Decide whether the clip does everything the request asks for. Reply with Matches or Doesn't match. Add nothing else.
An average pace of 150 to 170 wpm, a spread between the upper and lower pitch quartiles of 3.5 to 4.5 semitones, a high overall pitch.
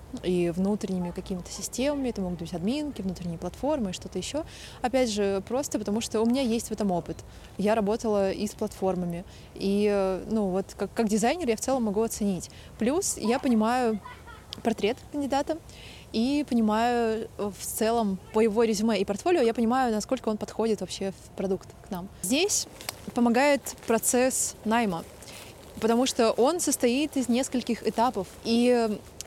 Matches